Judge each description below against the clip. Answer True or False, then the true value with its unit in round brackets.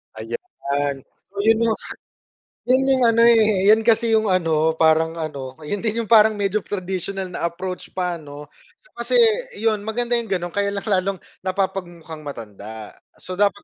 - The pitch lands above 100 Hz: True (190 Hz)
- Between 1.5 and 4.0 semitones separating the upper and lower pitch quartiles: False (5.3 semitones)